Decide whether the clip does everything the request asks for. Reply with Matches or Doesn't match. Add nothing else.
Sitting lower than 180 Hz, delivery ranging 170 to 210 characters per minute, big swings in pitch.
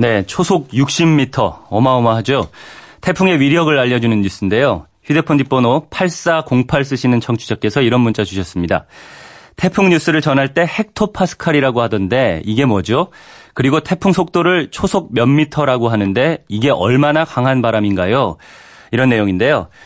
Doesn't match